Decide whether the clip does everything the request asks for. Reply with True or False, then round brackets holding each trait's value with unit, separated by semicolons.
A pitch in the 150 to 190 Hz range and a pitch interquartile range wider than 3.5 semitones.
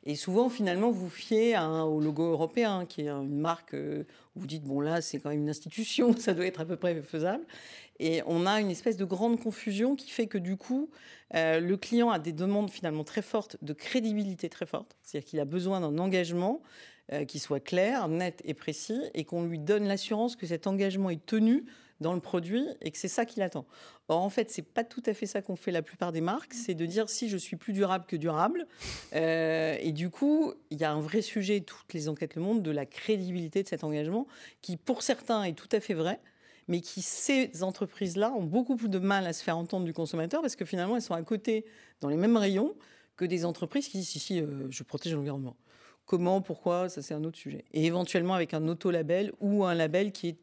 True (185 Hz; 5.2 semitones)